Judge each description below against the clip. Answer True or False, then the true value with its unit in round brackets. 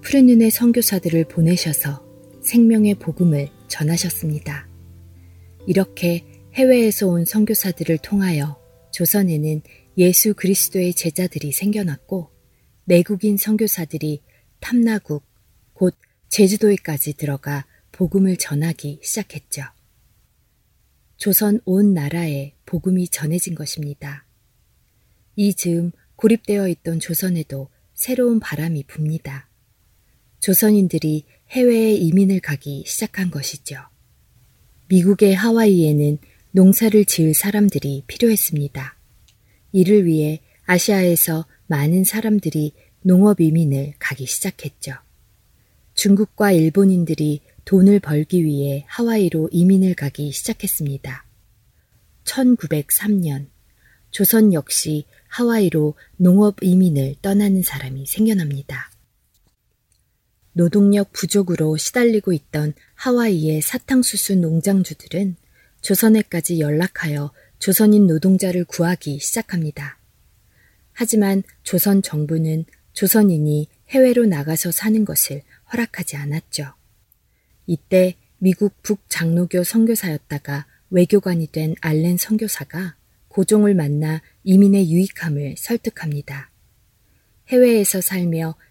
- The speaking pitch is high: False (170 Hz)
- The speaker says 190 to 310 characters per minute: True (255 characters per minute)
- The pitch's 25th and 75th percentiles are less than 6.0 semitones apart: True (5.2 semitones)